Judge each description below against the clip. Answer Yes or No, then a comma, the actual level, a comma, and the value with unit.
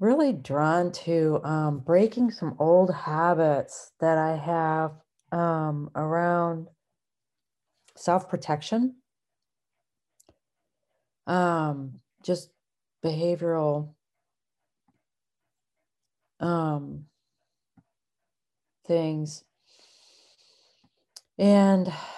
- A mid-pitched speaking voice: Yes, medium, 165 Hz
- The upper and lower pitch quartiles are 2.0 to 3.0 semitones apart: Yes, narrow, 2.6 semitones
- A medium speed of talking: No, slow, 55 wpm